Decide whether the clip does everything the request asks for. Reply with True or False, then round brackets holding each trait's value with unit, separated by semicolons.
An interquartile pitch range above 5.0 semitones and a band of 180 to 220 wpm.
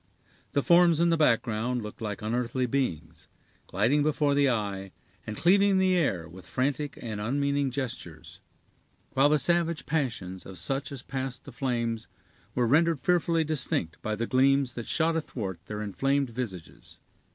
False (5.4 semitones; 155 wpm)